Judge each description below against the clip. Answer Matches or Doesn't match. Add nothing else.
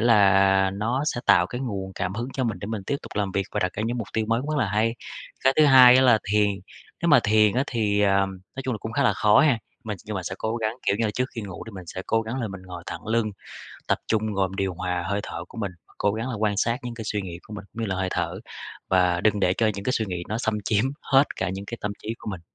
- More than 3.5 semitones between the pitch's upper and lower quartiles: Doesn't match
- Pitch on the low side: Matches